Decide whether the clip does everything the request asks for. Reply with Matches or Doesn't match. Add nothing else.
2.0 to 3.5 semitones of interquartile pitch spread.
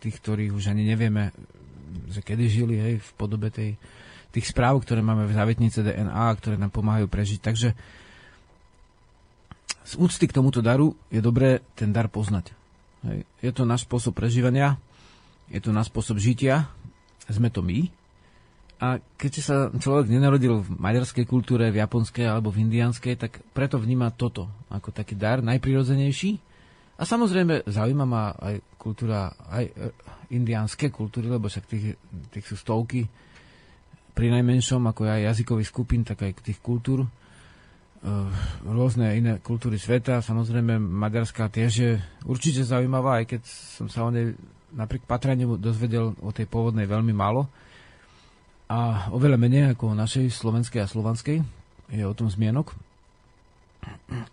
Matches